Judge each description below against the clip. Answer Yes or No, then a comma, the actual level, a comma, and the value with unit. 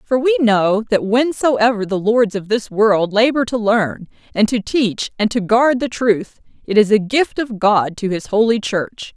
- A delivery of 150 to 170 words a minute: No, fast, 205 wpm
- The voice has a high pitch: Yes, high, 220 Hz